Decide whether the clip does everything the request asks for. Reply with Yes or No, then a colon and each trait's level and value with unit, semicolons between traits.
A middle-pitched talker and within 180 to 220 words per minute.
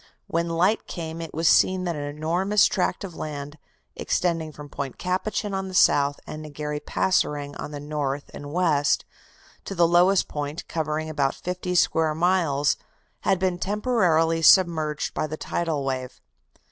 No: medium, 160 Hz; average, 160 wpm